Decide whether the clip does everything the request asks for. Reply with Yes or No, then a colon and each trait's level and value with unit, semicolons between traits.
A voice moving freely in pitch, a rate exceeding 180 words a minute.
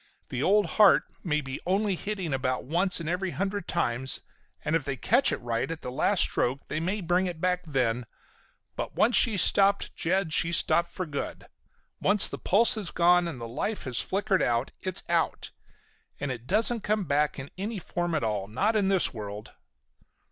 Yes: wide, 6.6 semitones; average, 190 wpm